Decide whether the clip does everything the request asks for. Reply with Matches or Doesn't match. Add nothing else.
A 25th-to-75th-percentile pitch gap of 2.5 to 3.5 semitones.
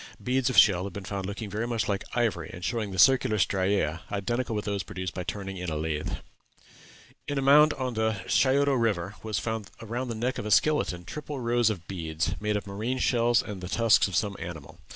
Doesn't match